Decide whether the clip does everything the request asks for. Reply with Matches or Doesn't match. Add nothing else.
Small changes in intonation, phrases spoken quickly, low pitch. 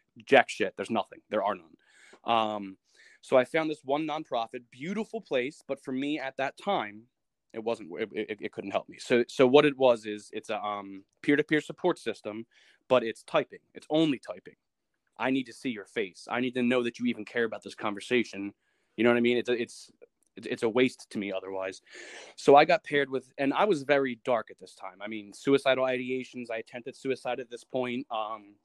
Doesn't match